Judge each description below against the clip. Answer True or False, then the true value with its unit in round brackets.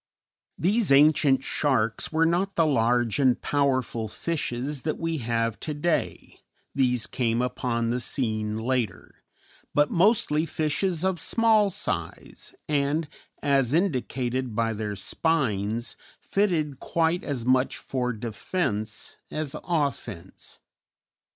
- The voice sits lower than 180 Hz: True (135 Hz)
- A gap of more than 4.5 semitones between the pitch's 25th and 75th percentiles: True (5.5 semitones)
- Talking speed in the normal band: False (115 wpm)